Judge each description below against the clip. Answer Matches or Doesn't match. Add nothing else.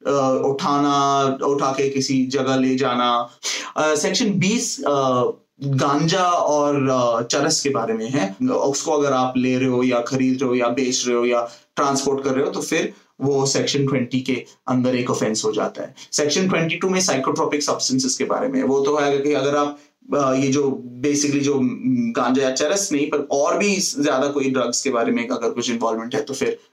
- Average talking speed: Doesn't match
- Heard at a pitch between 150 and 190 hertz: Doesn't match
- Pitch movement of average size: Doesn't match